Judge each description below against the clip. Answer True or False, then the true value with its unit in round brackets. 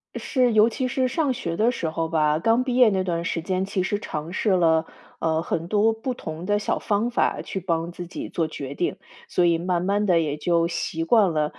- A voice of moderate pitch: True (180 Hz)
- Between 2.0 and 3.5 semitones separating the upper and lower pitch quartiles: False (4.6 semitones)